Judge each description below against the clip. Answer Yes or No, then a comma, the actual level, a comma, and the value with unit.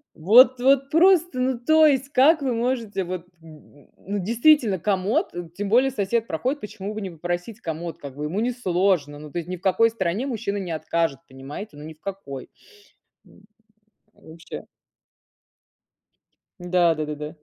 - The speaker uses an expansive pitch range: Yes, wide, 6.9 semitones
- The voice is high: Yes, high, 195 Hz